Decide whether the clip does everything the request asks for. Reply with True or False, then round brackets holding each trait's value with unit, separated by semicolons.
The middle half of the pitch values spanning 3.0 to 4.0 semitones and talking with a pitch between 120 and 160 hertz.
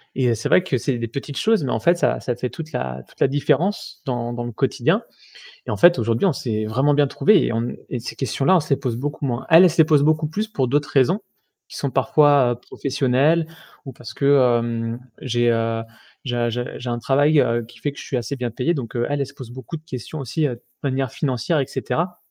True (3.7 semitones; 135 Hz)